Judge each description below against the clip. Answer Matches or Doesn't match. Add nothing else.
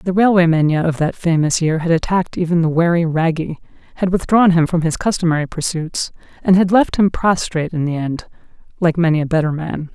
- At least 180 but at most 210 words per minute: Matches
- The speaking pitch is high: Doesn't match